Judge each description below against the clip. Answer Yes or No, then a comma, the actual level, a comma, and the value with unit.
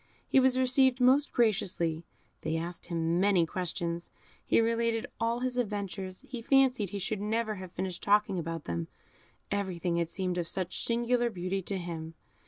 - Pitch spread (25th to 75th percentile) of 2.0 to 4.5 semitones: No, average, 5.2 semitones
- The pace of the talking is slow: No, average, 165 wpm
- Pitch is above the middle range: Yes, high, 195 Hz